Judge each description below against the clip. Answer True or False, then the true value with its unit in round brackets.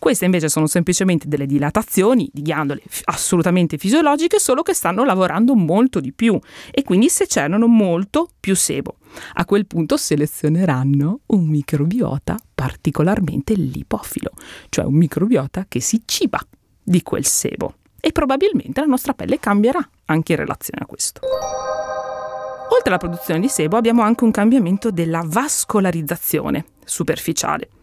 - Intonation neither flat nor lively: False (6.8 semitones)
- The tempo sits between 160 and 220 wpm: False (140 wpm)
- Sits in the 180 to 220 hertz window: True (185 Hz)